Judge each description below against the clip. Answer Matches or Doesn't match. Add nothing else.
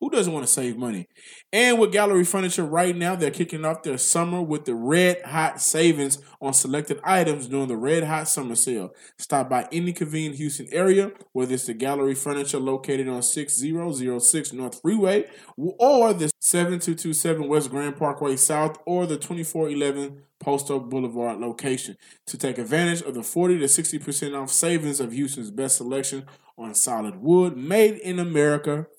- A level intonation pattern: Doesn't match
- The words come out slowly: Doesn't match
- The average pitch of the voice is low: Doesn't match